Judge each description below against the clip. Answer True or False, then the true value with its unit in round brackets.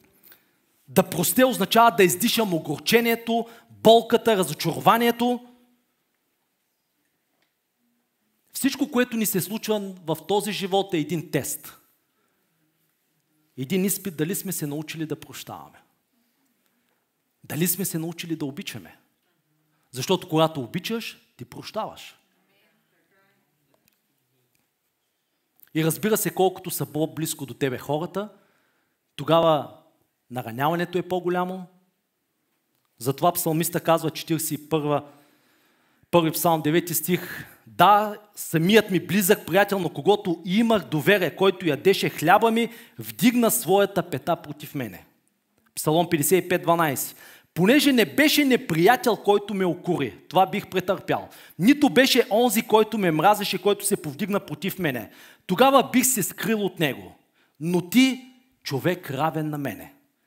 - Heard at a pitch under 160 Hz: False (180 Hz)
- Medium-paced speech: False (110 wpm)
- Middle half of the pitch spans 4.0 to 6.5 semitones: True (5.1 semitones)